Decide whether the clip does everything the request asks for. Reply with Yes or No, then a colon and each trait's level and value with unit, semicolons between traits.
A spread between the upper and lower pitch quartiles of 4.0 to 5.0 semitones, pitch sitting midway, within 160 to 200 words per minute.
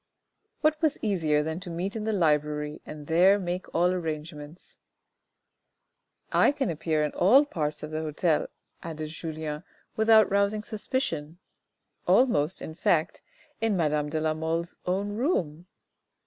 No: average, 4.7 semitones; medium, 165 Hz; average, 150 wpm